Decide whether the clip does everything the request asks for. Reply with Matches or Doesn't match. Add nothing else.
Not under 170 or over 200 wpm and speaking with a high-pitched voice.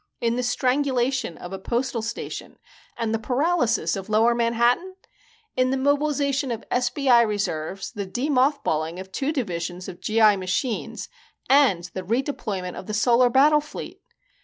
Doesn't match